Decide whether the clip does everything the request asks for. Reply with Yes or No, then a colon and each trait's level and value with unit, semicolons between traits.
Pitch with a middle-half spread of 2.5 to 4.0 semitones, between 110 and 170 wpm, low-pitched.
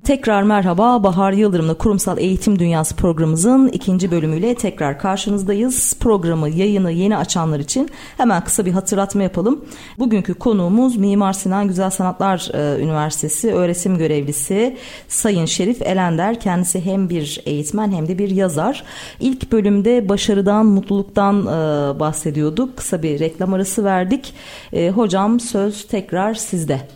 No: average, 3.7 semitones; average, 125 wpm; high, 195 Hz